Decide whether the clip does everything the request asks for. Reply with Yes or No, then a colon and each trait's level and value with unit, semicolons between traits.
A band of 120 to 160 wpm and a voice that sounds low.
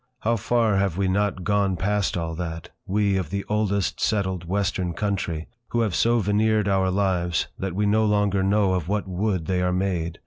No: average, 185 wpm; very low, 95 Hz